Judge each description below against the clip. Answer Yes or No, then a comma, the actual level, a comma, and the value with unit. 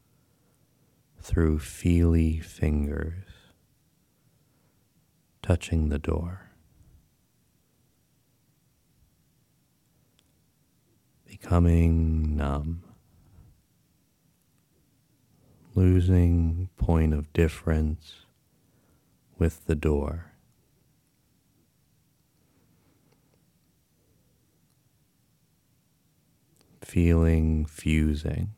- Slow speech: Yes, slow, 35 wpm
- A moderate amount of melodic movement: Yes, average, 3.4 semitones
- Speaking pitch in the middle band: No, very low, 85 Hz